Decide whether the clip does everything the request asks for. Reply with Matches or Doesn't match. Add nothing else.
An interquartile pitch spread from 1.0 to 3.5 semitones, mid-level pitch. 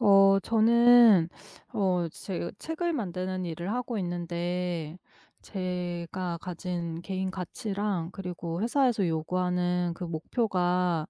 Matches